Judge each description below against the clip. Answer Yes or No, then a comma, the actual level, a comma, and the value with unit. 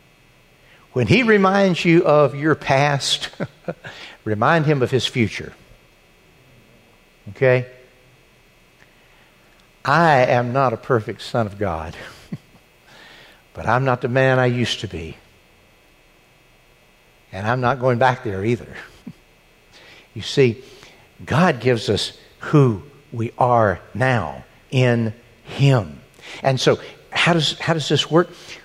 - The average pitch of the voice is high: No, low, 125 Hz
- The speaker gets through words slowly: Yes, slow, 115 wpm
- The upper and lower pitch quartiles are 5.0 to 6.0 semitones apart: No, average, 4.2 semitones